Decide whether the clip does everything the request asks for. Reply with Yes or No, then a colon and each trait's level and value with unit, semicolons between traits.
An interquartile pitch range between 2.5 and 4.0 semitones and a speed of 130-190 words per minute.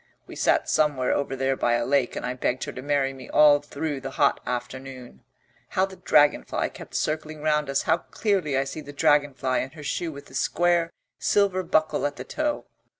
No: average, 2.8 semitones; fast, 205 wpm